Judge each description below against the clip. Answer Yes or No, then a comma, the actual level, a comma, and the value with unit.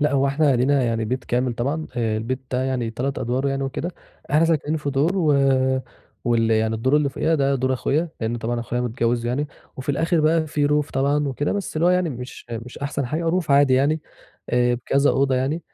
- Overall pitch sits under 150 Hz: Yes, low, 135 Hz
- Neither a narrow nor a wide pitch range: Yes, average, 3.3 semitones